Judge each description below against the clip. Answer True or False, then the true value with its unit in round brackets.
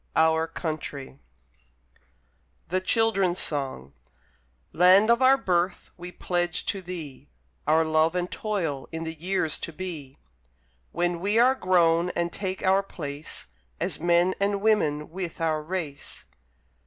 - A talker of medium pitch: True (175 Hz)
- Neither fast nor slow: False (130 wpm)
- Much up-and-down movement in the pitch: False (3.1 semitones)